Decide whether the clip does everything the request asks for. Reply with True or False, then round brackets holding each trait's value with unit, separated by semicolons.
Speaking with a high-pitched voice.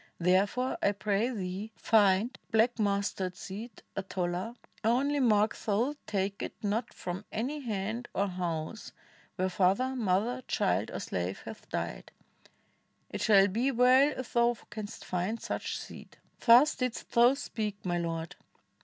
True (215 Hz)